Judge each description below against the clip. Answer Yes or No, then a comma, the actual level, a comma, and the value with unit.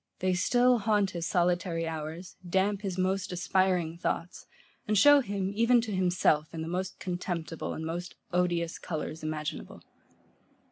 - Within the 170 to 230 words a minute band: No, average, 145 wpm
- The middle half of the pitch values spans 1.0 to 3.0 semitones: Yes, average, 2.7 semitones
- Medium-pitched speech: Yes, medium, 180 Hz